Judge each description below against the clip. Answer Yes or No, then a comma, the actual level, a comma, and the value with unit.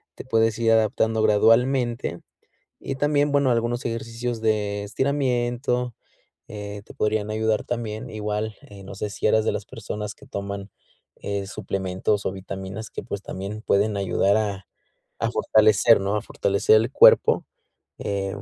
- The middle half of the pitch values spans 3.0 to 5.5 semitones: No, narrow, 2.5 semitones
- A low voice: Yes, low, 110 Hz